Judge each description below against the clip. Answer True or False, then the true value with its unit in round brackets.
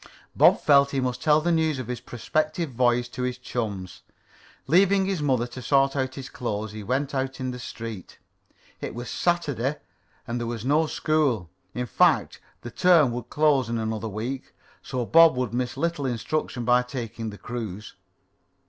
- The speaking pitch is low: True (125 Hz)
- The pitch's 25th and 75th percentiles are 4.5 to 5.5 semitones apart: False (3.7 semitones)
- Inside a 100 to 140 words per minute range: False (175 wpm)